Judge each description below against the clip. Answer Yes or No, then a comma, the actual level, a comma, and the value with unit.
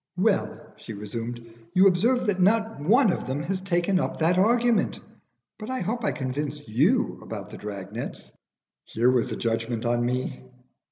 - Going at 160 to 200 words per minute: Yes, average, 170 wpm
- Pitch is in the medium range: Yes, medium, 160 Hz